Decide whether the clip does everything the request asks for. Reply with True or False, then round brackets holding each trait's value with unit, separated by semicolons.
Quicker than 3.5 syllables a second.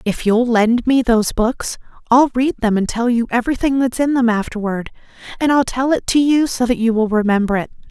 True (5.6 syllables/s)